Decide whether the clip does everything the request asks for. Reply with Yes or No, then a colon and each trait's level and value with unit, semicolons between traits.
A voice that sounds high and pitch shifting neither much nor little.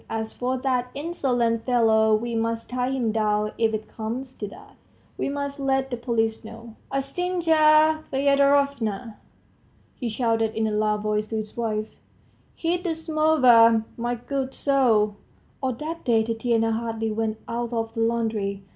Yes: high, 235 Hz; average, 3.6 semitones